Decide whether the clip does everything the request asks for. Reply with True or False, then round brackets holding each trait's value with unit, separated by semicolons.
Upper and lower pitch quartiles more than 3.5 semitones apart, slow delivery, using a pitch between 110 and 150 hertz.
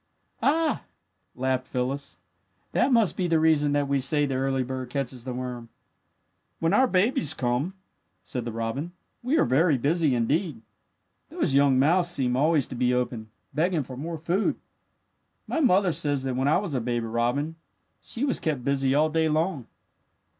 False (4.6 semitones; 175 wpm; 140 Hz)